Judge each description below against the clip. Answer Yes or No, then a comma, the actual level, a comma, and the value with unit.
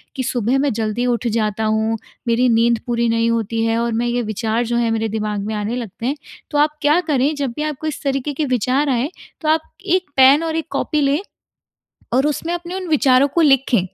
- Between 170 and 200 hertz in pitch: No, very high, 250 Hz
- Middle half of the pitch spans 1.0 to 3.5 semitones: No, average, 4.4 semitones